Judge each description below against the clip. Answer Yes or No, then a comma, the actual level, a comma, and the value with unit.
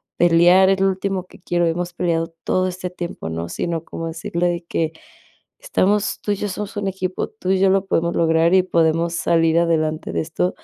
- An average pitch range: No, narrow, 2.3 semitones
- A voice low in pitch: No, medium, 175 Hz